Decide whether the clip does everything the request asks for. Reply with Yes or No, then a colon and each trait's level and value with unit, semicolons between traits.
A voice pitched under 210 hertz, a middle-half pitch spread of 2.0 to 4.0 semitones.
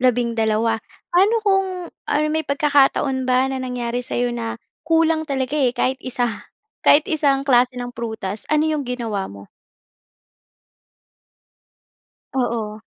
No: very high, 255 Hz; average, 3.5 semitones